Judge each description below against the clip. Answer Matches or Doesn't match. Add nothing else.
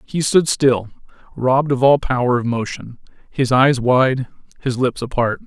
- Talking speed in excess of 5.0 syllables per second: Doesn't match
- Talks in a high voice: Doesn't match